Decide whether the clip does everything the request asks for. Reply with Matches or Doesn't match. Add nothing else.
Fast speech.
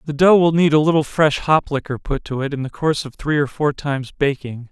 Matches